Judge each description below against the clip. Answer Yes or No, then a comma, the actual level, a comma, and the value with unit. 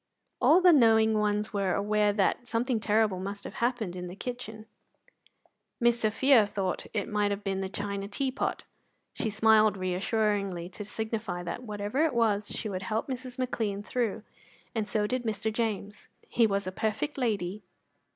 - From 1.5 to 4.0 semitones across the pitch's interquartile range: Yes, narrow, 2.4 semitones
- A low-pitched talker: No, high, 215 Hz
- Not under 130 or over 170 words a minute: Yes, average, 165 wpm